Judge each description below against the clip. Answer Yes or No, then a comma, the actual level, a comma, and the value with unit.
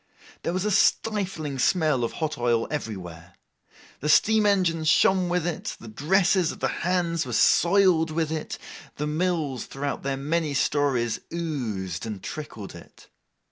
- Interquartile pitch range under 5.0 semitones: No, wide, 5.5 semitones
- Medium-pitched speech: Yes, medium, 155 Hz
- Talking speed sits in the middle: Yes, average, 150 wpm